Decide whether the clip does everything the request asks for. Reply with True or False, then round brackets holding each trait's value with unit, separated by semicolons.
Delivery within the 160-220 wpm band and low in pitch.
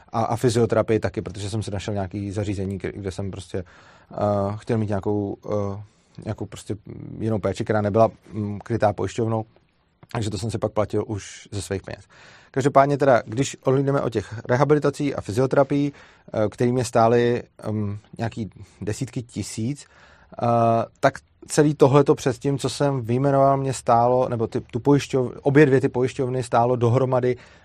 True (165 wpm; 115 Hz)